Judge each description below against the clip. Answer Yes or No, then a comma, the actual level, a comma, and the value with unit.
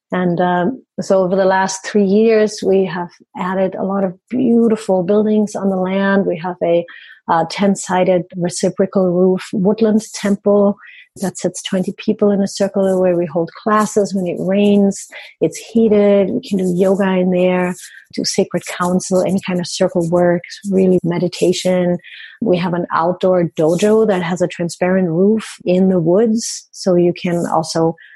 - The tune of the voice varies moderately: No, narrow, 2.1 semitones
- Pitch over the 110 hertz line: Yes, high, 190 Hz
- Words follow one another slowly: No, average, 165 wpm